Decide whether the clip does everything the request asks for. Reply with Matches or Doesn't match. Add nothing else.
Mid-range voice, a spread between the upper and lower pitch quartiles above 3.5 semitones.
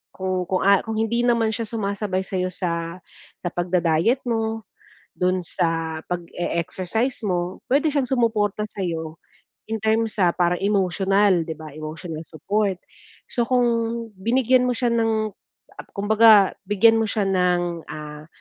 Doesn't match